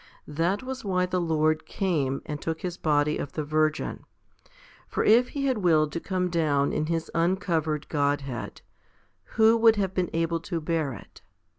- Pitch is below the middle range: No, medium, 165 Hz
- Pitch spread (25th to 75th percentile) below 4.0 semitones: Yes, average, 3.4 semitones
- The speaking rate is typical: Yes, average, 170 wpm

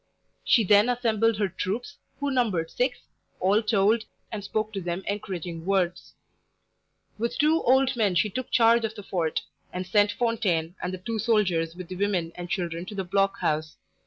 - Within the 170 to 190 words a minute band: Yes, average, 180 wpm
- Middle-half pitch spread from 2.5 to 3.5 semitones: No, average, 4.1 semitones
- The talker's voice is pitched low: No, high, 200 Hz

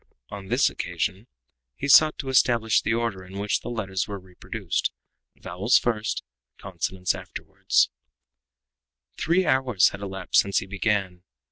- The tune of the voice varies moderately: Yes, average, 3.8 semitones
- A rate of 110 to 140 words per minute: Yes, slow, 135 wpm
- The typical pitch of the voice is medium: No, low, 100 Hz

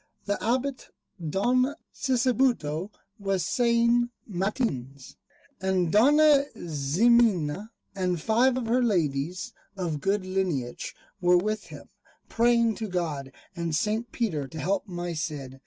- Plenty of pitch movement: Yes, wide, 6.4 semitones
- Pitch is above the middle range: Yes, high, 195 Hz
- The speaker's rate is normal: No, slow, 120 wpm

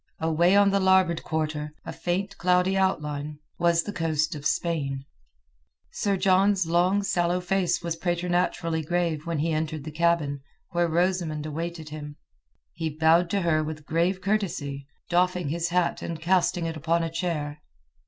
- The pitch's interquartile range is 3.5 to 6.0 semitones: No, narrow, 2.5 semitones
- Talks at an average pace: Yes, average, 160 wpm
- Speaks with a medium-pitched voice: Yes, medium, 170 Hz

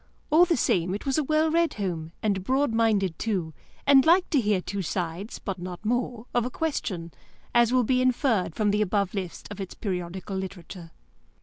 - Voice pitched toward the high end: Yes, high, 210 Hz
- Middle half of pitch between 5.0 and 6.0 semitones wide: Yes, wide, 5.6 semitones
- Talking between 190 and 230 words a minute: Yes, average, 195 wpm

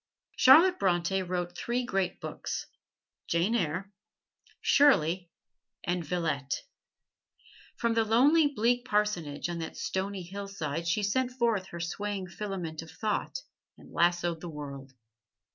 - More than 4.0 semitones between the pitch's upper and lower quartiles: Yes, average, 4.9 semitones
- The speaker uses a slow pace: Yes, slow, 125 wpm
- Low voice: No, high, 190 Hz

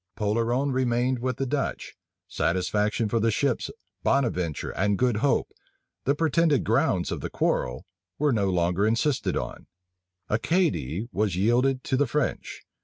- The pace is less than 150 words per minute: Yes, average, 140 wpm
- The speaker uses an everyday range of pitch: Yes, average, 4.8 semitones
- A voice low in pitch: Yes, low, 120 Hz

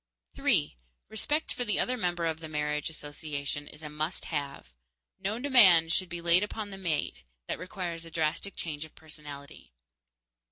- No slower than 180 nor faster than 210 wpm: No, average, 165 wpm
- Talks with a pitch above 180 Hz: No, medium, 165 Hz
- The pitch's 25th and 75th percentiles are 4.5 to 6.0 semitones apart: No, average, 4.0 semitones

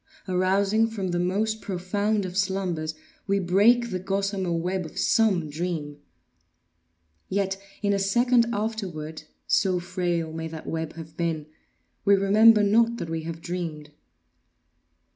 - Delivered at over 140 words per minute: No, slow, 135 wpm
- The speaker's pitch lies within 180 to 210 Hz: Yes, medium, 185 Hz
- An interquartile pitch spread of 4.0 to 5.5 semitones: No, average, 3.4 semitones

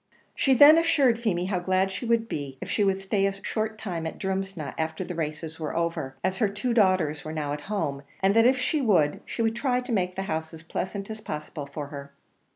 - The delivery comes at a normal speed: No, fast, 235 wpm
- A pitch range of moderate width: No, wide, 5.7 semitones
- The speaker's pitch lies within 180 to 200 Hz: Yes, high, 190 Hz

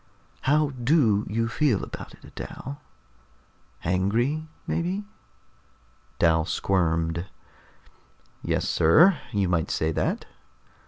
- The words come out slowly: Yes, slow, 95 wpm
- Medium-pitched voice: No, low, 105 Hz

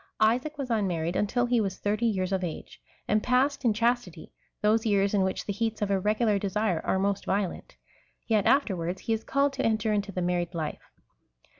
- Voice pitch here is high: Yes, high, 210 Hz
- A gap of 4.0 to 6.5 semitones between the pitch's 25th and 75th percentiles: No, average, 3.3 semitones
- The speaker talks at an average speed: Yes, average, 190 wpm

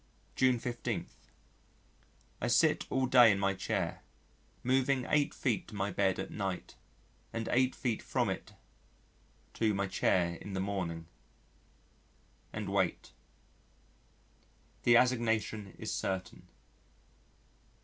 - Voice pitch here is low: Yes, low, 105 Hz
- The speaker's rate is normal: No, slow, 115 wpm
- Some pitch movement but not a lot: Yes, average, 4.3 semitones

